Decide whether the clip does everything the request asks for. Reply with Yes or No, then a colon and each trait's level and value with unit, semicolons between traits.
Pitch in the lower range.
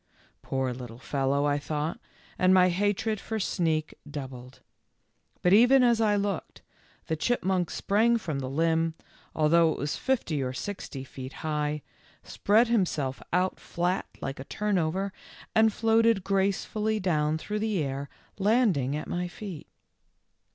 No: medium, 175 Hz